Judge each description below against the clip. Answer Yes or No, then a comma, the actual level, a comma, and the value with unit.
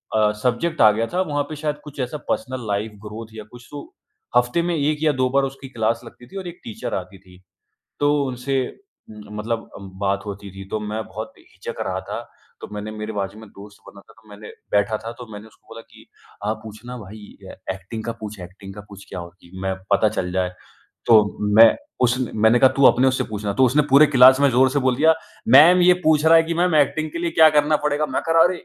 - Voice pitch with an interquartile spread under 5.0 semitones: No, wide, 5.4 semitones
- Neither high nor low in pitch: No, low, 115 Hz